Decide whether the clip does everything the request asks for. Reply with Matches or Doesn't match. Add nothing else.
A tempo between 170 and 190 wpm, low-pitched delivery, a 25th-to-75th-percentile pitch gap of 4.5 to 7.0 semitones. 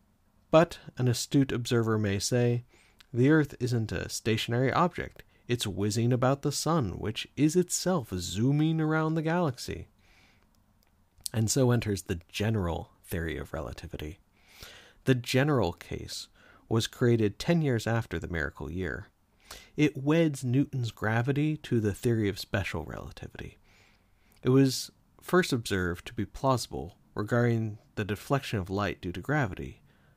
Doesn't match